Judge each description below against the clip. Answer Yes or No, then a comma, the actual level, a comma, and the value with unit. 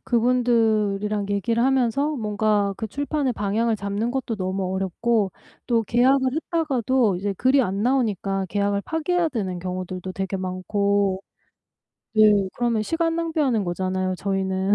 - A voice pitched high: Yes, high, 210 Hz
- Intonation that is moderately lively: Yes, average, 4.3 semitones